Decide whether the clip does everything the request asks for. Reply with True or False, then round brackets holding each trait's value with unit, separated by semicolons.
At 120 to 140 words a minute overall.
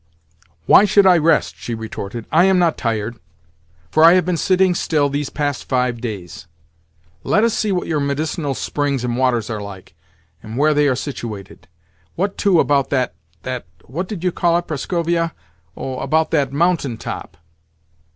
False (165 wpm)